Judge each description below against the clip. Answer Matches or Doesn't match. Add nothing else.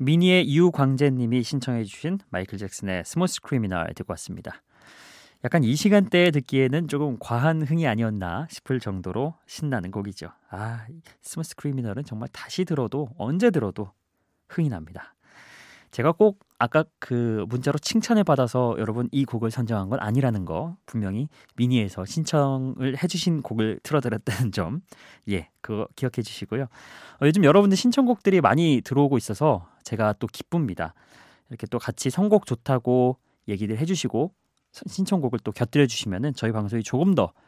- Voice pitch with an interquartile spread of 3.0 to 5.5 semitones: Doesn't match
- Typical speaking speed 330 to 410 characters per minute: Matches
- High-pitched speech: Doesn't match